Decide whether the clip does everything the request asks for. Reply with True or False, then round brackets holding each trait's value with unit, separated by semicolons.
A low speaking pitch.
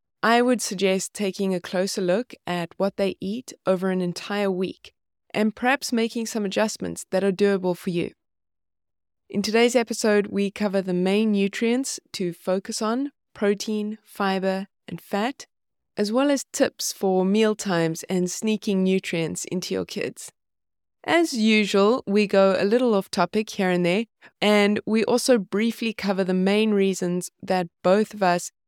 False (200 Hz)